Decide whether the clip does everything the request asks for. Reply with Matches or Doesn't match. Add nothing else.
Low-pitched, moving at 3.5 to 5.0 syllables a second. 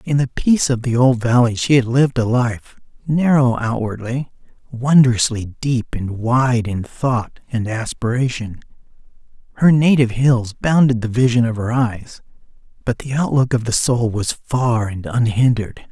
Matches